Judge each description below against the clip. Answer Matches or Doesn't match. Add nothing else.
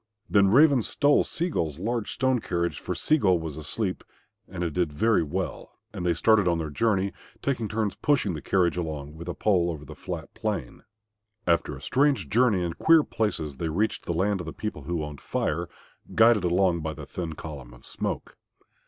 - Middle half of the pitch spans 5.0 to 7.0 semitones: Matches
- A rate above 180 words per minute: Matches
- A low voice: Matches